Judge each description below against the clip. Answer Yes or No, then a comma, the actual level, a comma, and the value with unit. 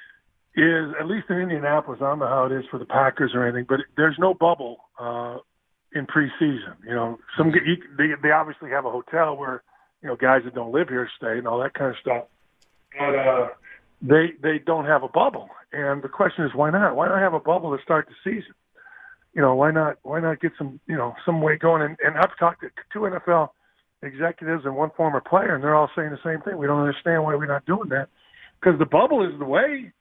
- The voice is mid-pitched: Yes, medium, 155 Hz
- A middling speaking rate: No, fast, 235 wpm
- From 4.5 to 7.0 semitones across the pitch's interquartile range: No, average, 3.5 semitones